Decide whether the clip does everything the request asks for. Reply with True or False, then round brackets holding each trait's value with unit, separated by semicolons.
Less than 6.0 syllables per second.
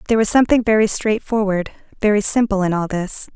False (6.3 syllables/s)